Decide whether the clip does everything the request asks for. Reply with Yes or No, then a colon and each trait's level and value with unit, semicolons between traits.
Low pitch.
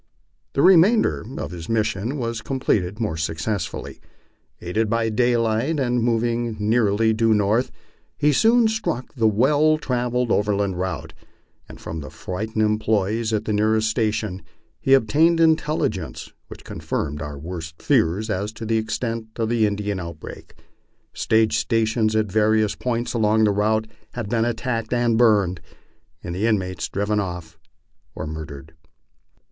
Yes: low, 110 Hz